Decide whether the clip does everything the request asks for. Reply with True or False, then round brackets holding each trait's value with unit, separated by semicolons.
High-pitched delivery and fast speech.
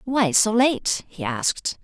False (220 Hz; 165 wpm)